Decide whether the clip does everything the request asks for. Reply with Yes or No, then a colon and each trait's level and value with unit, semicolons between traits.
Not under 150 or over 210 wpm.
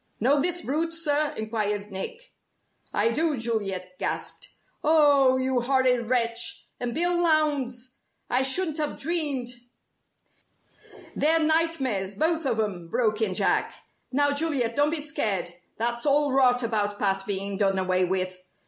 No: average, 140 wpm